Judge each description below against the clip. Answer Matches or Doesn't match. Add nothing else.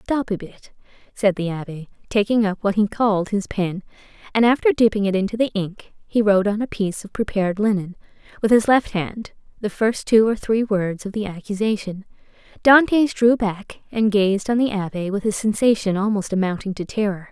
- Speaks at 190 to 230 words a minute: Matches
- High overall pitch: Matches